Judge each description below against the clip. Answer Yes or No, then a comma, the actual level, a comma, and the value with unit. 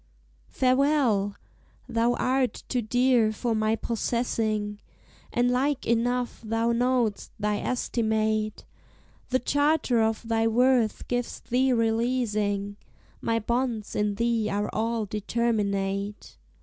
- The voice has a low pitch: No, high, 230 Hz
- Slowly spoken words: Yes, slow, 110 wpm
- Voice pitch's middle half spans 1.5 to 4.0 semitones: Yes, narrow, 2.5 semitones